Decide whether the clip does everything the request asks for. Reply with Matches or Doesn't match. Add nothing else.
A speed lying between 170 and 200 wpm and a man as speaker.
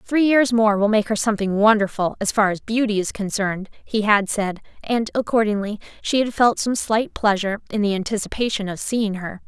Doesn't match